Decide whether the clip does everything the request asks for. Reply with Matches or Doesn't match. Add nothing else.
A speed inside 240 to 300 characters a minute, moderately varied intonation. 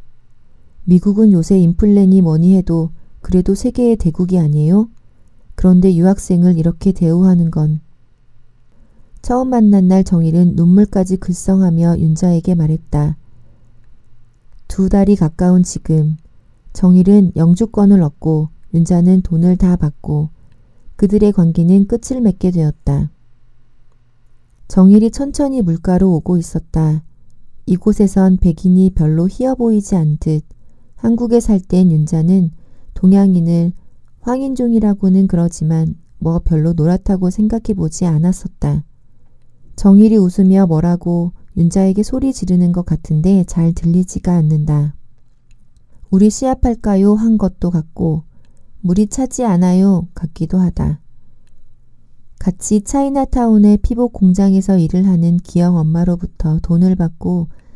Matches